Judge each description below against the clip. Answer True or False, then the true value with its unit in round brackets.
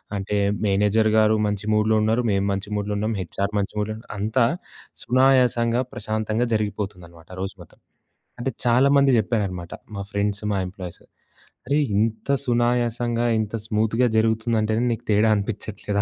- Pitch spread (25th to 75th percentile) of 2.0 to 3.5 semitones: True (2.6 semitones)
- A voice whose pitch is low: True (110 Hz)